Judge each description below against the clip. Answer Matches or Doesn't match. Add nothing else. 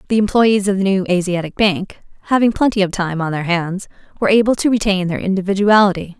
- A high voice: Matches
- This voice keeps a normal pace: Matches